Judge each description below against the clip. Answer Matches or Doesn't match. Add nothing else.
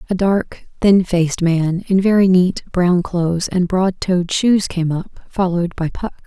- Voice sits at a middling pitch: Matches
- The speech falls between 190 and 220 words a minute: Doesn't match